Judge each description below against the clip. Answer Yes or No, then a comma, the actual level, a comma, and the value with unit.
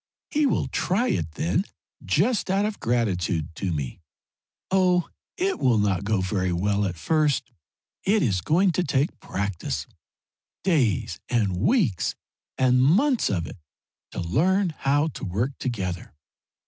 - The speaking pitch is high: No, low, 120 Hz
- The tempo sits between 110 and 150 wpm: Yes, average, 140 wpm